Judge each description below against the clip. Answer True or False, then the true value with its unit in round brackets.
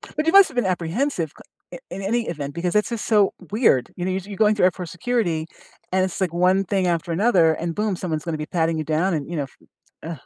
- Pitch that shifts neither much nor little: True (4.2 semitones)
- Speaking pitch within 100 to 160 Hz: False (180 Hz)